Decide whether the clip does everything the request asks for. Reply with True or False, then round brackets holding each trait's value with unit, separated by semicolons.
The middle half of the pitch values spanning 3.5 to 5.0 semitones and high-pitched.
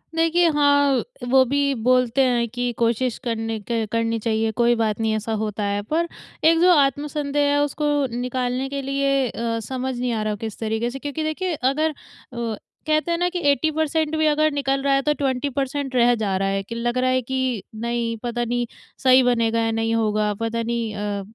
True (3.8 semitones; 250 Hz)